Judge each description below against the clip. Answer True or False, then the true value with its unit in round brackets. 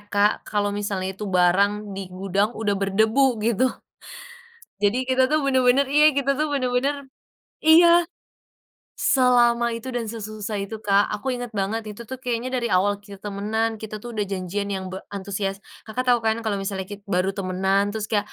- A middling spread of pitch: True (3.8 semitones)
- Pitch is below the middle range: False (215 Hz)